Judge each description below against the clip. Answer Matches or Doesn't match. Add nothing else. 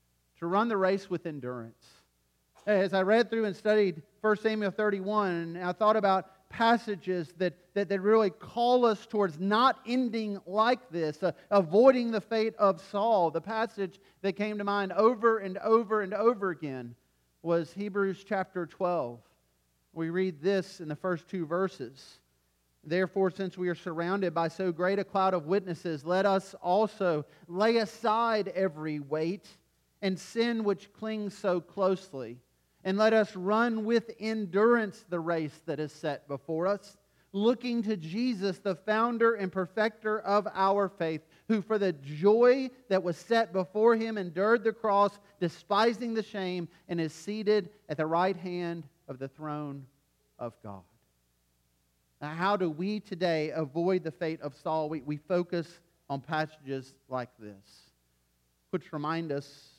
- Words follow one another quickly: Doesn't match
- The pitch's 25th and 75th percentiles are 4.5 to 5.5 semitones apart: Matches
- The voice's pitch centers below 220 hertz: Matches